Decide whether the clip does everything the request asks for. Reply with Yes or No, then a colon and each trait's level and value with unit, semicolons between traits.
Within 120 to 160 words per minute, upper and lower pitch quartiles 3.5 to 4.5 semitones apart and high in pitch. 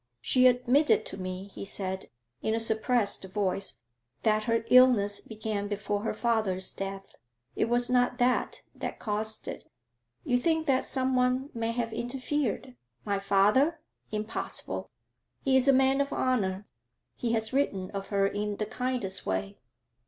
Yes: average, 150 wpm; average, 4.1 semitones; high, 220 Hz